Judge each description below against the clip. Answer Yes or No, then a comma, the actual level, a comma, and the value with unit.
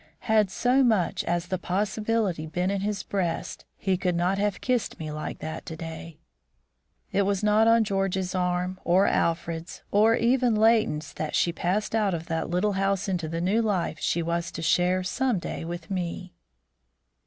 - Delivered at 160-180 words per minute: Yes, average, 175 wpm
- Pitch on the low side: No, medium, 185 Hz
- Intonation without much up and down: No, average, 3.6 semitones